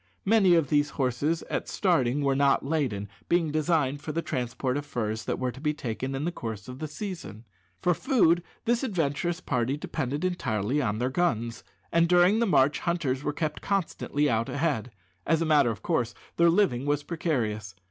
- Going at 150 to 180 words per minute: No, average, 190 wpm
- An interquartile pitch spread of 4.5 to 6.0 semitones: Yes, average, 5.1 semitones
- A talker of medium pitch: Yes, medium, 145 Hz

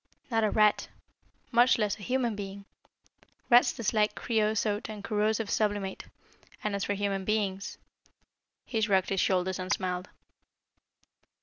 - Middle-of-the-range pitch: No, high, 210 Hz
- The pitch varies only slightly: Yes, narrow, 2.0 semitones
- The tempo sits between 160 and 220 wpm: No, slow, 135 wpm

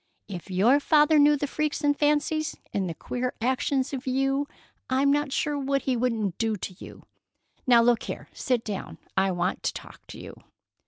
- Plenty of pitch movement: No, average, 4.4 semitones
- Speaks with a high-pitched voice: Yes, very high, 260 Hz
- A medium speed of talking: Yes, average, 190 wpm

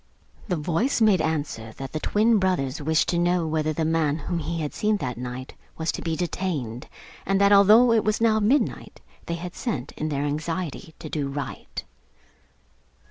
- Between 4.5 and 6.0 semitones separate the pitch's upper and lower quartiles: Yes, average, 4.9 semitones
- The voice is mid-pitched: Yes, medium, 165 Hz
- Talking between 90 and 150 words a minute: No, average, 185 wpm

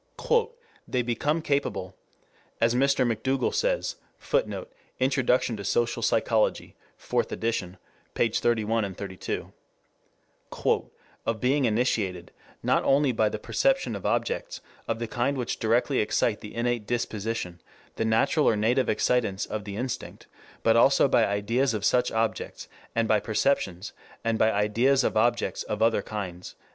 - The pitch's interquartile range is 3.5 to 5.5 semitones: No, average, 3.1 semitones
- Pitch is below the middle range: Yes, low, 115 Hz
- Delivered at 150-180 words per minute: No, average, 140 wpm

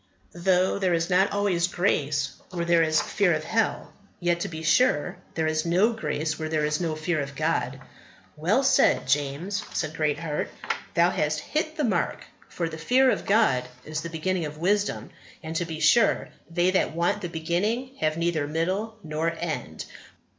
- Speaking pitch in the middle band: Yes, medium, 170 Hz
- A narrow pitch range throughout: No, average, 3.6 semitones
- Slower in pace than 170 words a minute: No, average, 180 wpm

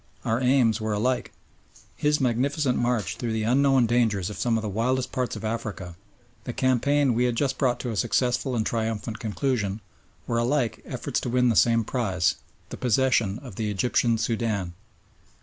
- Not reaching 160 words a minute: No, average, 175 wpm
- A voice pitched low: Yes, low, 120 Hz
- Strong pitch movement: No, average, 2.7 semitones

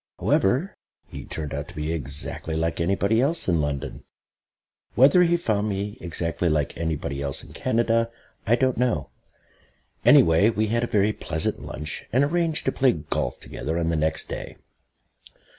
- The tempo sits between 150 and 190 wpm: Yes, average, 160 wpm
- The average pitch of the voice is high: No, low, 100 Hz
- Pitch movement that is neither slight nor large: No, wide, 7.1 semitones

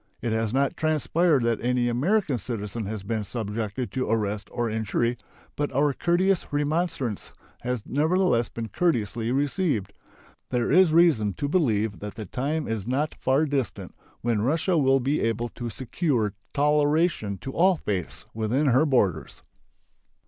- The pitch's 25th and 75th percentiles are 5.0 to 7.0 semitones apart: Yes, average, 5.3 semitones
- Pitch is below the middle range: Yes, low, 125 Hz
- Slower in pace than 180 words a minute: Yes, average, 150 wpm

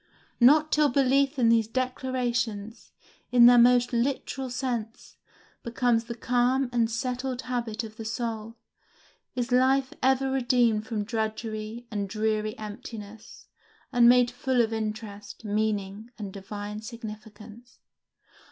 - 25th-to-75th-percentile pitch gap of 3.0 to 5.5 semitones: No, narrow, 2.5 semitones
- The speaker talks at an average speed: No, slow, 125 wpm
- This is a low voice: No, high, 235 Hz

